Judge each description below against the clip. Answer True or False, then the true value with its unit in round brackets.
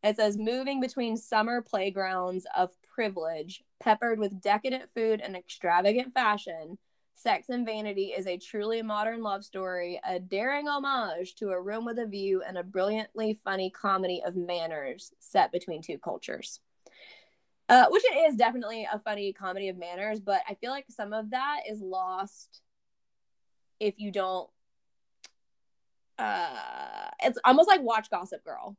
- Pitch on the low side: False (210 Hz)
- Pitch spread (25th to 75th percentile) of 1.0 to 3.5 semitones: False (4.1 semitones)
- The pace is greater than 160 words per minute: False (150 wpm)